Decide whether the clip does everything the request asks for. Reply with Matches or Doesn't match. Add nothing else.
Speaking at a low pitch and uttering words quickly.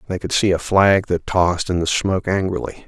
Matches